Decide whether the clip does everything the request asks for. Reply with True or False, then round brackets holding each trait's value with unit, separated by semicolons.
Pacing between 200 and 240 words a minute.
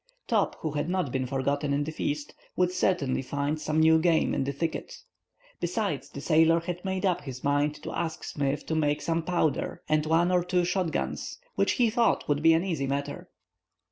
True (205 wpm)